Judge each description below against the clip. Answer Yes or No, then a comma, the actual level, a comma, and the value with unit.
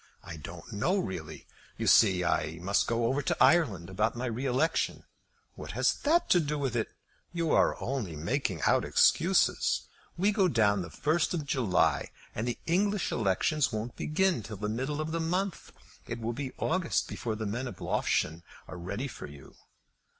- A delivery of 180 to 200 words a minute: Yes, average, 185 wpm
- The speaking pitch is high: No, low, 120 Hz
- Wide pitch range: Yes, wide, 7.9 semitones